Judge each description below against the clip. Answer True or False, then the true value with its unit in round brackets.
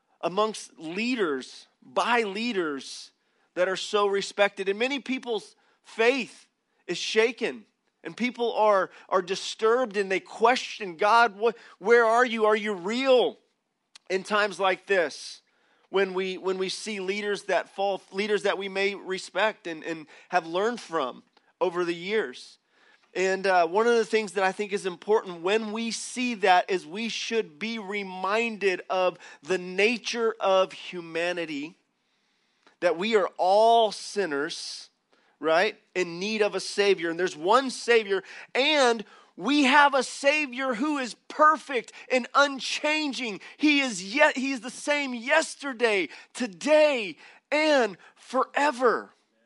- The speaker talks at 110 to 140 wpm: True (135 wpm)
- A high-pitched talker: True (215 Hz)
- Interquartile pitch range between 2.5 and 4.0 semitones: False (4.7 semitones)